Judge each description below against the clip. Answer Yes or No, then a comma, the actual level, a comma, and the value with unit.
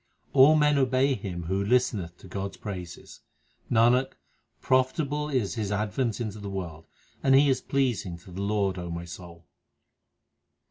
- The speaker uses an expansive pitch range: Yes, wide, 6.0 semitones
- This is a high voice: No, low, 105 Hz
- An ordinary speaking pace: Yes, average, 155 wpm